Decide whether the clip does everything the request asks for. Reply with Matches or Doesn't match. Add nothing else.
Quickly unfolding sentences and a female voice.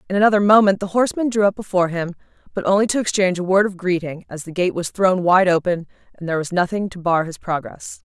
Matches